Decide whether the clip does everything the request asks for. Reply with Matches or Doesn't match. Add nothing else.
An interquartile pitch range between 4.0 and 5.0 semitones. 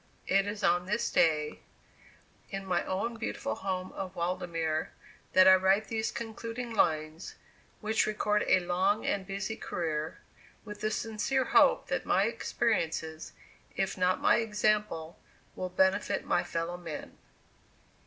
Doesn't match